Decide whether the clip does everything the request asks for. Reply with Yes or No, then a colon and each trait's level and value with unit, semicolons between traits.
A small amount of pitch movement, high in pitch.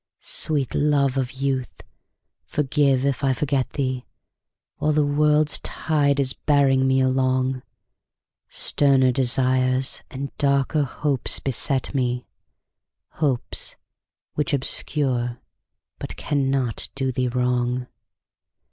No: narrow, 1.8 semitones; low, 135 Hz